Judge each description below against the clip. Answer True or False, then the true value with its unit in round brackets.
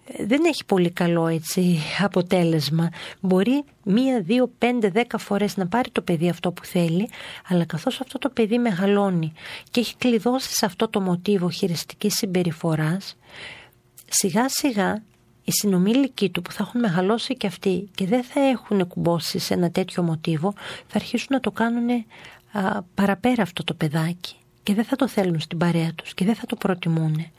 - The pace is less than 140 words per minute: False (165 wpm)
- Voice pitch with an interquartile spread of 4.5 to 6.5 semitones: True (5.0 semitones)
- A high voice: True (195 Hz)